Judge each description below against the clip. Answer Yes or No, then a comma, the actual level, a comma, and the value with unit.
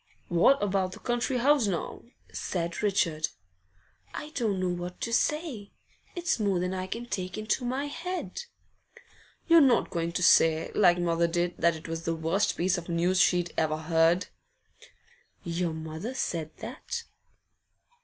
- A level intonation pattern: No, wide, 5.6 semitones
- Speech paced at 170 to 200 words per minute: No, average, 155 wpm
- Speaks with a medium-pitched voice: Yes, medium, 180 Hz